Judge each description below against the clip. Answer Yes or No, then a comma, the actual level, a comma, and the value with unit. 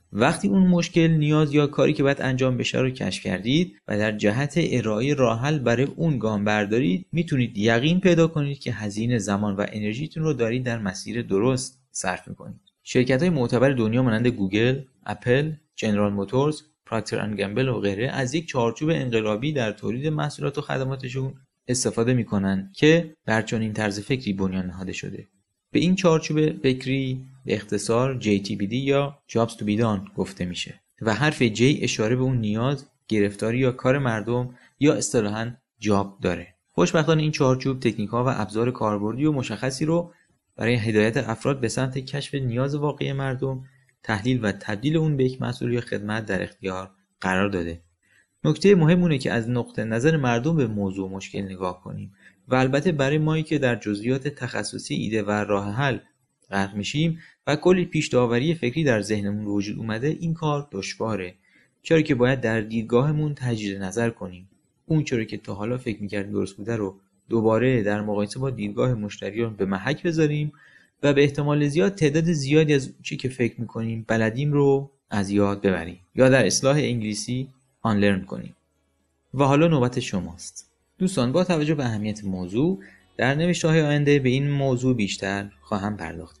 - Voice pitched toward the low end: Yes, low, 125 Hz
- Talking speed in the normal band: No, fast, 170 wpm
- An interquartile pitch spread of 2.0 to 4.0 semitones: No, wide, 5.4 semitones